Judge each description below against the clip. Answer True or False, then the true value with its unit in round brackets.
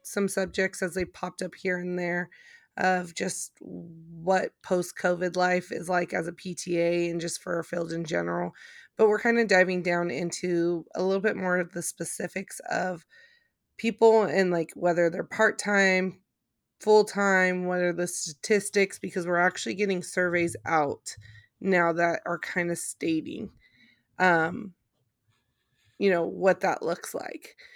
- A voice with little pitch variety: True (2.2 semitones)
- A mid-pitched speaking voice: True (180 Hz)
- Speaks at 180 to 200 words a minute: False (160 wpm)